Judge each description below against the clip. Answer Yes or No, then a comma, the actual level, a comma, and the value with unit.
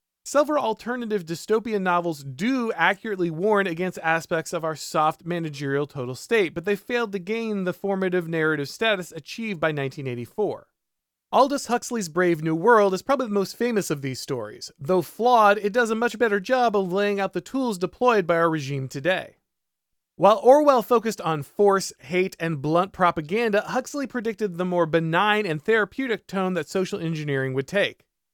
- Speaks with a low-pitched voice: No, high, 190 Hz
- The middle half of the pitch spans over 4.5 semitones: Yes, average, 5.2 semitones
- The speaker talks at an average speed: Yes, average, 170 wpm